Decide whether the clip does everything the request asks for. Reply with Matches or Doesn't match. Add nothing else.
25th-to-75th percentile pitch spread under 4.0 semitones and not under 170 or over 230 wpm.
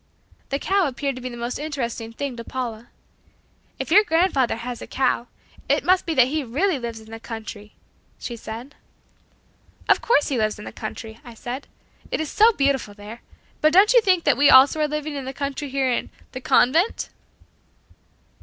Doesn't match